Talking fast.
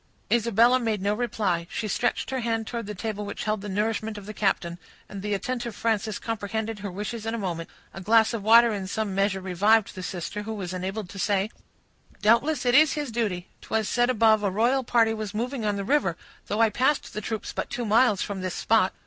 Yes: fast, 220 wpm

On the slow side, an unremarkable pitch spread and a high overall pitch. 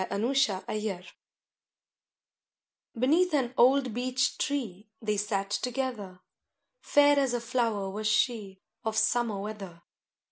Yes: slow, 120 wpm; average, 4.0 semitones; high, 225 Hz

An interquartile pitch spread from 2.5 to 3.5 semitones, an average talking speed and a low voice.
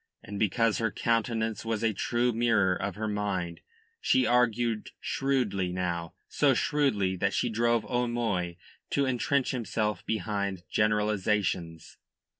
No: average, 3.1 semitones; slow, 125 wpm; low, 110 Hz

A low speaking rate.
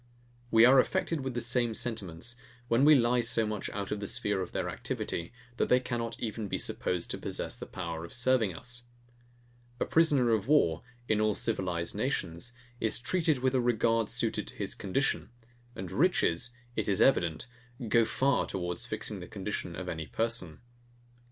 No: average, 175 wpm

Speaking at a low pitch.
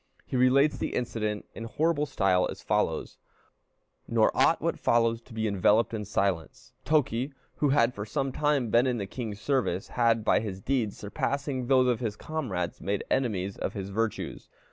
Yes: low, 115 Hz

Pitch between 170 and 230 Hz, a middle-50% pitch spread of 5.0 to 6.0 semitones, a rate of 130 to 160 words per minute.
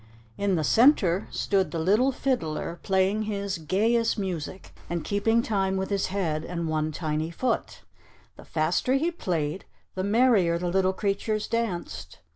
No: high, 190 Hz; average, 4.3 semitones; average, 150 wpm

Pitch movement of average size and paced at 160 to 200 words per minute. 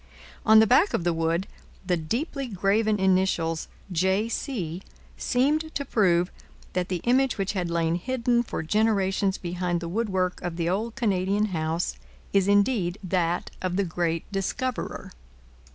No: average, 4.2 semitones; average, 150 wpm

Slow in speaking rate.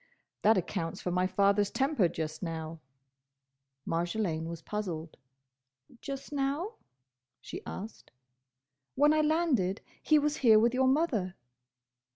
Yes: slow, 120 wpm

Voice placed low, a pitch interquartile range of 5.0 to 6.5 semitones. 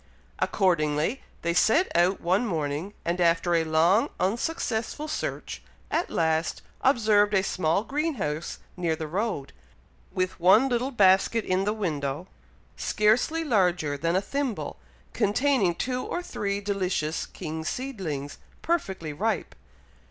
No: high, 190 Hz; wide, 5.5 semitones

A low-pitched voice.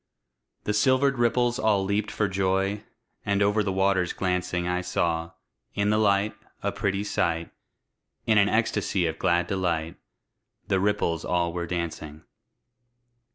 Yes: very low, 95 Hz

